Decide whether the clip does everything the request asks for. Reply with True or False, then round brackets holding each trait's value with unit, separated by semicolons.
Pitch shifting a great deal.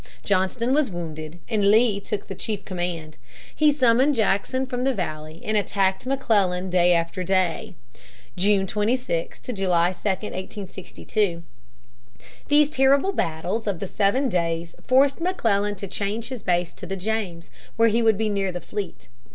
False (4.5 semitones)